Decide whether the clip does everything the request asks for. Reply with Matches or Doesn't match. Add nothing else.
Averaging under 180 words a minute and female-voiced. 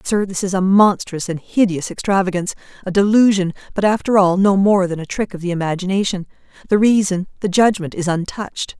Doesn't match